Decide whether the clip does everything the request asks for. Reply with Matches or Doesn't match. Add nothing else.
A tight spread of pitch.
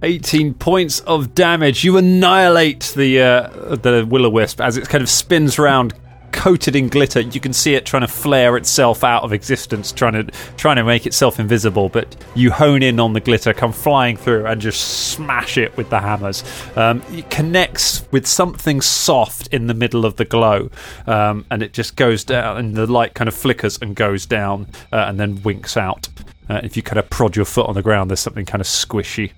Doesn't match